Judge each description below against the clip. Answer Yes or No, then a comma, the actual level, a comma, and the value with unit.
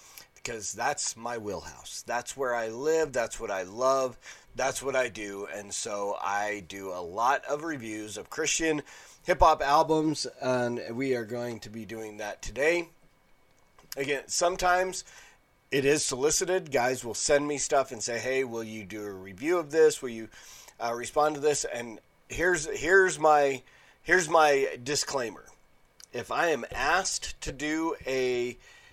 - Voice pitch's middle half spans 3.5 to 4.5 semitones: No, wide, 5.4 semitones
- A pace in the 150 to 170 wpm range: Yes, average, 160 wpm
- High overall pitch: No, low, 130 Hz